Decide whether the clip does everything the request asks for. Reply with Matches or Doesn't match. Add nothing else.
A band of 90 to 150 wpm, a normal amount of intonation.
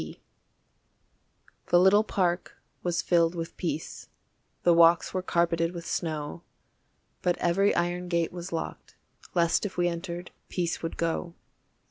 Doesn't match